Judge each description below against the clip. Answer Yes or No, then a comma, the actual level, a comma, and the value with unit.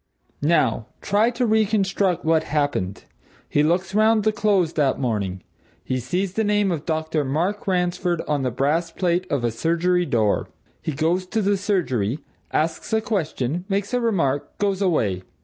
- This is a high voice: No, medium, 170 Hz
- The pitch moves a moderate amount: No, wide, 5.7 semitones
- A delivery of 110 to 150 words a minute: No, average, 165 wpm